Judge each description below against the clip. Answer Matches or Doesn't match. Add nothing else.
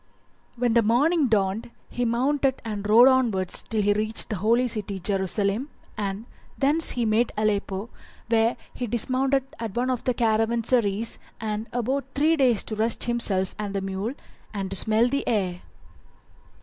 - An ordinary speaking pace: Matches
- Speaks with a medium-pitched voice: Doesn't match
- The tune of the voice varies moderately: Matches